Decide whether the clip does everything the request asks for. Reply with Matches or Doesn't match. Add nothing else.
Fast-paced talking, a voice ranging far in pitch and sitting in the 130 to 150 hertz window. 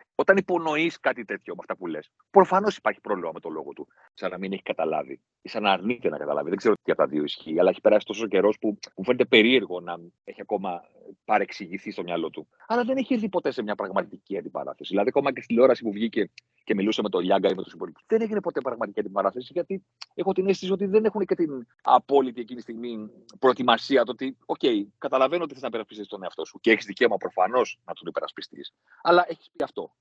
Matches